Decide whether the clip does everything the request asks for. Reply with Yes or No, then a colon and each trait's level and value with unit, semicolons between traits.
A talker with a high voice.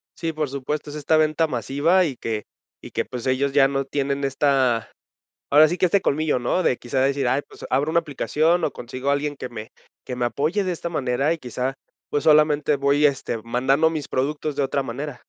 No: medium, 140 Hz